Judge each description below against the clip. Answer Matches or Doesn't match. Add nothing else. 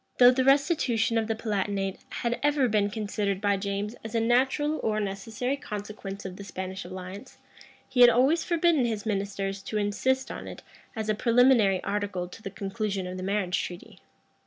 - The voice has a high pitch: Matches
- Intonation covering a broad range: Doesn't match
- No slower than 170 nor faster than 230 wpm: Matches